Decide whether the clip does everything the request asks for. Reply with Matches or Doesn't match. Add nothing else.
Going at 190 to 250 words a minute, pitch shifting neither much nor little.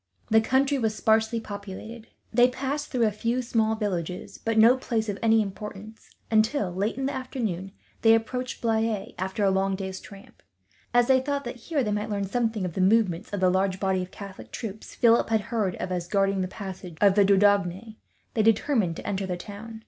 Matches